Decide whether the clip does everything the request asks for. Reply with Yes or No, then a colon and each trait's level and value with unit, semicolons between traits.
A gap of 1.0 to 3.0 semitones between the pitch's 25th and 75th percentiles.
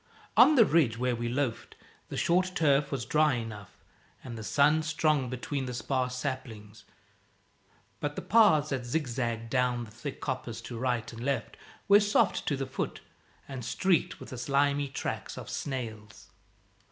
No: average, 3.8 semitones